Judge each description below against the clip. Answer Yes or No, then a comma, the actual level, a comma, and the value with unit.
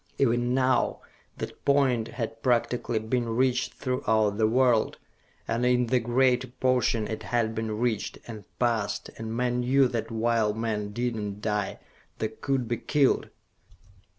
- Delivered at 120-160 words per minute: Yes, average, 150 wpm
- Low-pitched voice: Yes, low, 120 Hz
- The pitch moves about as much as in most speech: No, narrow, 2.2 semitones